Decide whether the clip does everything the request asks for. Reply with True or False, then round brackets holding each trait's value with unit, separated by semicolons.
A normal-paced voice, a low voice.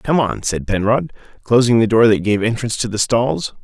False (215 wpm; 115 Hz)